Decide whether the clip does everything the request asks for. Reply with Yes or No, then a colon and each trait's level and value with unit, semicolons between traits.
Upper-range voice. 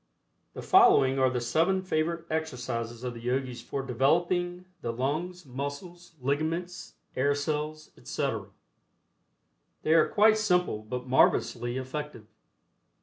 No: medium, 145 Hz